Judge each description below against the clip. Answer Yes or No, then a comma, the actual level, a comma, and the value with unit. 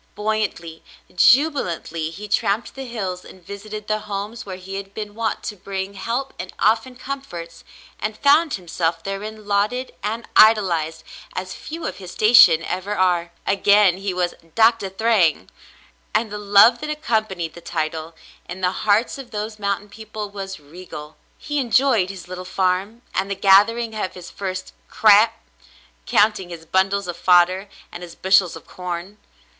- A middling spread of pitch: Yes, average, 3.2 semitones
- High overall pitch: Yes, high, 200 Hz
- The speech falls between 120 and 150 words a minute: No, average, 160 wpm